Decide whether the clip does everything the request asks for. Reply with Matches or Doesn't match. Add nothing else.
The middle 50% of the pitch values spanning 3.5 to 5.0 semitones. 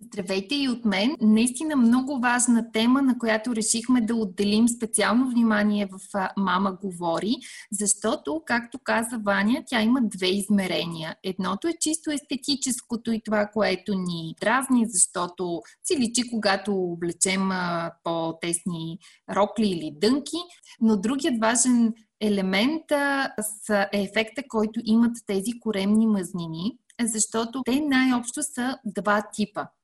Matches